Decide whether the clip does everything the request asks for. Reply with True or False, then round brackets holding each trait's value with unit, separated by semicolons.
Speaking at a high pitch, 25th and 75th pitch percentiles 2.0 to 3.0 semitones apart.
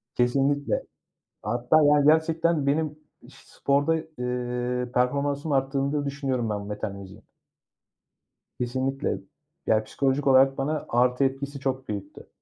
False (135 Hz; 2.6 semitones)